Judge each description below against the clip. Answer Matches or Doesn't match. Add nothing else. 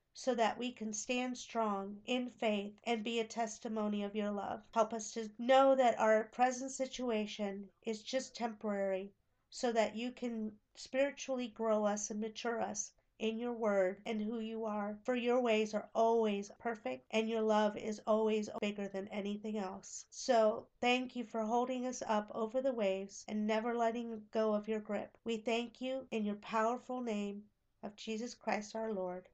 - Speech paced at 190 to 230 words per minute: Doesn't match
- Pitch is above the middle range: Matches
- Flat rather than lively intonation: Matches